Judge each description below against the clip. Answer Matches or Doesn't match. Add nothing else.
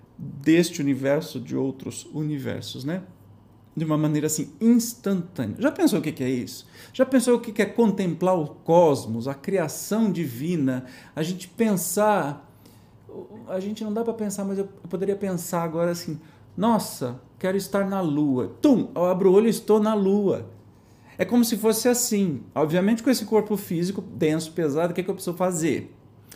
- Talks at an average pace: Matches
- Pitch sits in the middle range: Matches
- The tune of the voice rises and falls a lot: Matches